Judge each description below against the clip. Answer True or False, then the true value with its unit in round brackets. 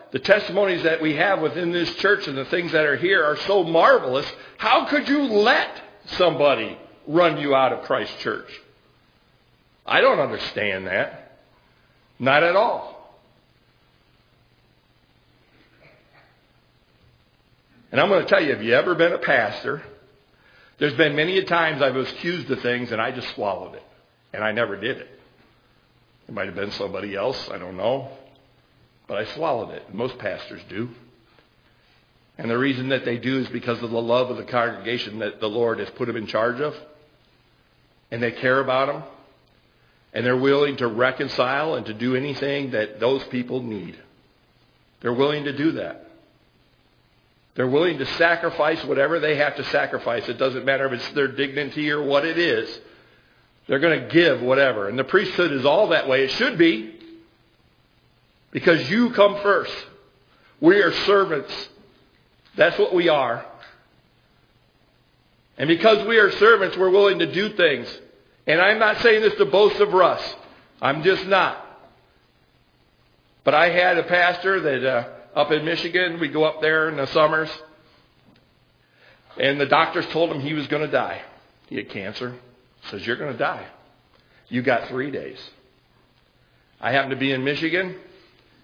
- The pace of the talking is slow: False (165 wpm)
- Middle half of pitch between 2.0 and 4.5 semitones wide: False (5.1 semitones)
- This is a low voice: False (145 Hz)